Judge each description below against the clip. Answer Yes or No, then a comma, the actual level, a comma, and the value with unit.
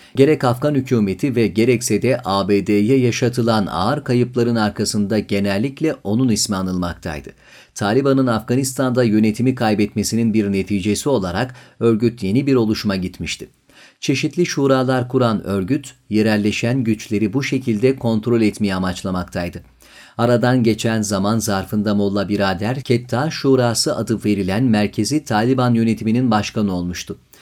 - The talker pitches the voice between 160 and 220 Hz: No, low, 110 Hz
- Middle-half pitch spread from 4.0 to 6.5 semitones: No, average, 3.6 semitones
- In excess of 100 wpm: Yes, average, 115 wpm